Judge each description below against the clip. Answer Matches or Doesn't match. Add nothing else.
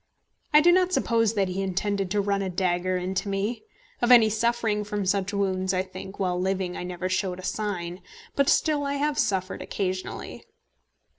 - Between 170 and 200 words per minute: Matches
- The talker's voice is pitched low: Doesn't match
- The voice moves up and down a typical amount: Matches